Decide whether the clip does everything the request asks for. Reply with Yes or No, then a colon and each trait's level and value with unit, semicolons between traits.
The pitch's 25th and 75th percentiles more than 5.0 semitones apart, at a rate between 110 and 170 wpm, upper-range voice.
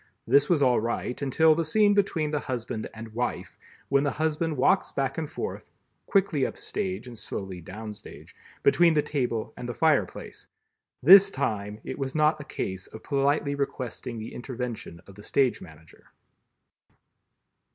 No: wide, 5.4 semitones; average, 165 wpm; low, 135 Hz